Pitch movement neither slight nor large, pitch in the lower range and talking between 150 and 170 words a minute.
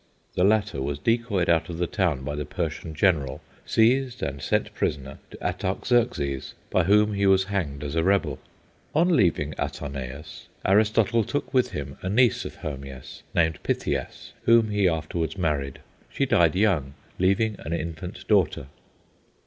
No: wide, 6.3 semitones; very low, 85 Hz; average, 155 wpm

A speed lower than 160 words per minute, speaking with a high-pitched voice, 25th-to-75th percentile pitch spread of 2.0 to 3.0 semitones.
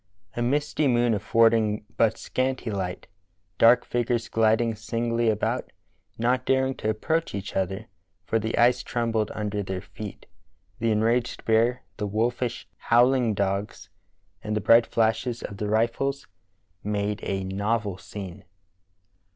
No: slow, 135 wpm; low, 115 Hz; narrow, 2.4 semitones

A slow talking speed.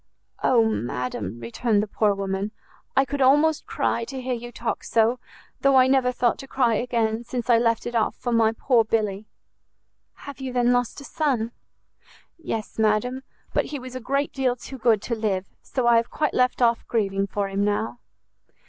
No: average, 190 wpm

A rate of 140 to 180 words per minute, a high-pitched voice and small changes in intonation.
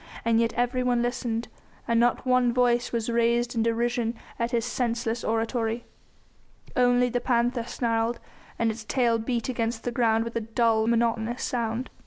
Yes: average, 160 wpm; high, 235 Hz; narrow, 1.1 semitones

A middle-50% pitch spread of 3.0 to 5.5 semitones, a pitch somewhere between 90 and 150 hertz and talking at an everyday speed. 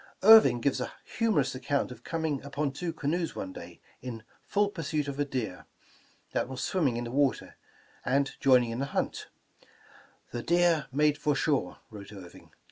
Yes: average, 3.8 semitones; medium, 140 Hz; average, 175 wpm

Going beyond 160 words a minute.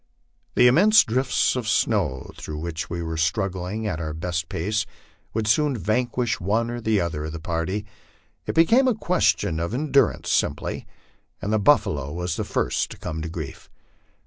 Yes: average, 170 wpm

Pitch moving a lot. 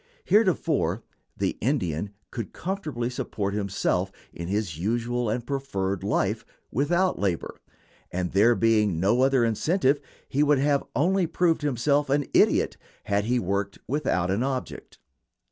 Yes: wide, 6.4 semitones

